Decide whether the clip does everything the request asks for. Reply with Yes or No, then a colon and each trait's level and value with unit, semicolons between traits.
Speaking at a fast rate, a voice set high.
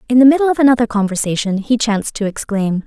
Yes: fast, 210 wpm; high, 230 Hz